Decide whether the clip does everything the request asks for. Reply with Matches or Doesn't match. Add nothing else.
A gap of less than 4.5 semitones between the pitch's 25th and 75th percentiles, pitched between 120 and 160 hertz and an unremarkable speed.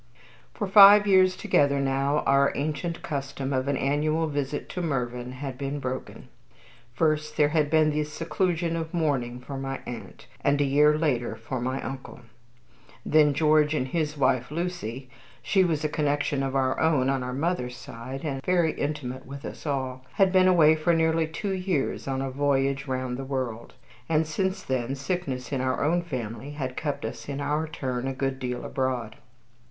Matches